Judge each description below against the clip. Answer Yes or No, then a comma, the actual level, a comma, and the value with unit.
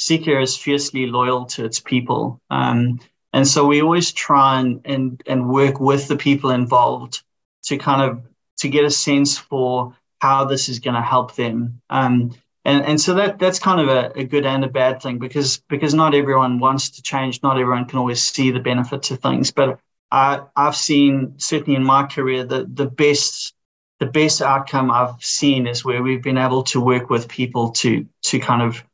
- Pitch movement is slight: Yes, narrow, 2.1 semitones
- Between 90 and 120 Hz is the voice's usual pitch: No, low, 135 Hz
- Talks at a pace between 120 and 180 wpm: No, average, 200 wpm